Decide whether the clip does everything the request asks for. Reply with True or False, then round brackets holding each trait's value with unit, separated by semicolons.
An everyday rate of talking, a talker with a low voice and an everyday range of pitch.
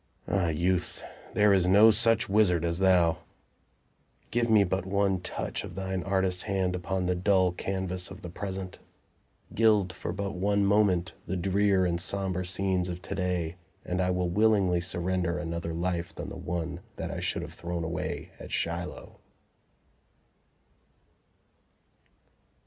False (150 wpm; 90 Hz; 1.9 semitones)